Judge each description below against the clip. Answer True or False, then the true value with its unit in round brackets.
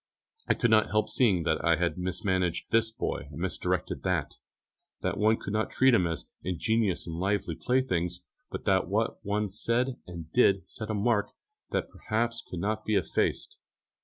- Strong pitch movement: False (3.9 semitones)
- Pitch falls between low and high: False (100 Hz)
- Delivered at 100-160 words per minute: False (175 wpm)